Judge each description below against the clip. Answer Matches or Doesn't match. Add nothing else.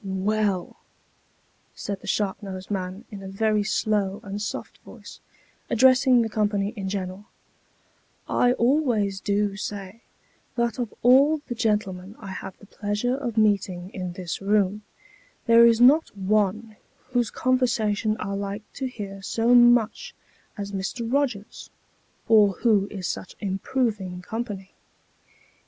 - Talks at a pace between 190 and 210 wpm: Doesn't match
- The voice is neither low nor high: Doesn't match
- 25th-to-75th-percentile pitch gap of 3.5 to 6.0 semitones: Doesn't match